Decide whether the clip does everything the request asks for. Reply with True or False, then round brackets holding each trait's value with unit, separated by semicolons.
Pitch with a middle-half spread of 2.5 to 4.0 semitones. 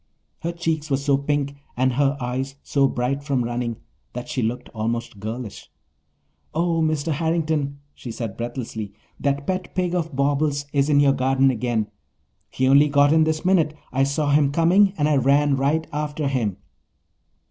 True (3.3 semitones)